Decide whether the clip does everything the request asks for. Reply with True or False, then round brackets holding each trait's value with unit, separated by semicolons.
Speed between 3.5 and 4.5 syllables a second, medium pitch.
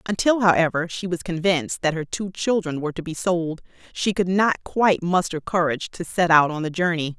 False (5.5 syllables/s; 175 Hz)